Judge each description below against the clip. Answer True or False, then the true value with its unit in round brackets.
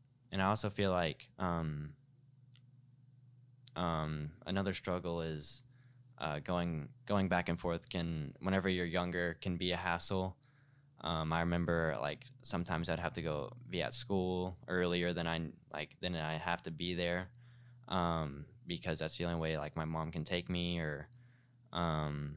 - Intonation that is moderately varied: True (4.6 semitones)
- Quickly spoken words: False (160 wpm)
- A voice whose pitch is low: True (90 Hz)